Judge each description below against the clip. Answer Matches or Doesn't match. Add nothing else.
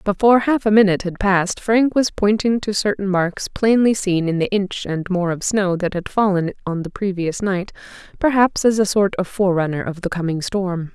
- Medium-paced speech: Doesn't match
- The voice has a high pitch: Matches